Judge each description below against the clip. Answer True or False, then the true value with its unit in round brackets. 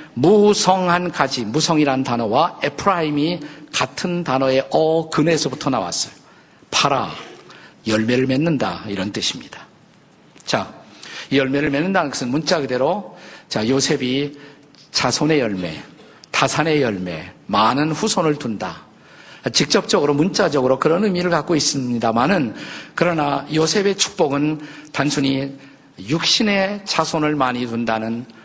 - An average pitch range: True (3.7 semitones)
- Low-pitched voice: False (145 Hz)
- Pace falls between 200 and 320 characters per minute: True (270 characters per minute)